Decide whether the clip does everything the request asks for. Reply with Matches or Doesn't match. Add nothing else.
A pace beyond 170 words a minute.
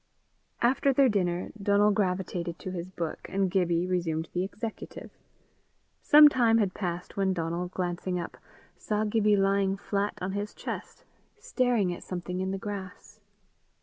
Doesn't match